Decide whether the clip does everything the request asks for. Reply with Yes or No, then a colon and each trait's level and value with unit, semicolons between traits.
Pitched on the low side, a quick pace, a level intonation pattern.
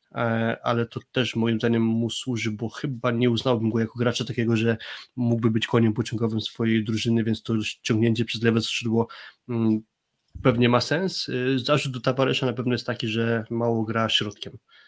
Yes: low, 115 Hz; fast, 170 wpm; narrow, 1.4 semitones